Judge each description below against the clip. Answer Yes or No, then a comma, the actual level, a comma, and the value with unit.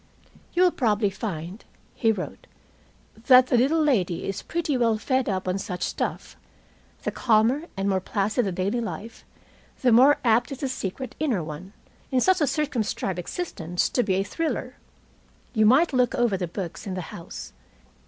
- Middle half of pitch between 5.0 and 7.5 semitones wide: Yes, average, 5.3 semitones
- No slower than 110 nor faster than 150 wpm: No, average, 175 wpm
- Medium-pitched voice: No, high, 225 Hz